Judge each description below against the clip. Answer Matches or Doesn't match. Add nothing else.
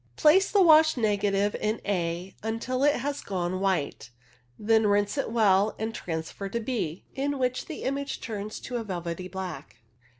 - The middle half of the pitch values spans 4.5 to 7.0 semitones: Matches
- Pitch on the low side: Doesn't match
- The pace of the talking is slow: Doesn't match